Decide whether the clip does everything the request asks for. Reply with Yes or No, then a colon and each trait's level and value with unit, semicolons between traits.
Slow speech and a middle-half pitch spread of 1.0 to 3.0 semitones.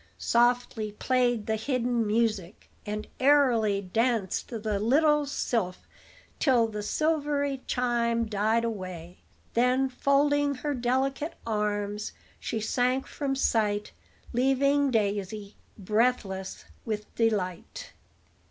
No: slow, 100 wpm; average, 4.0 semitones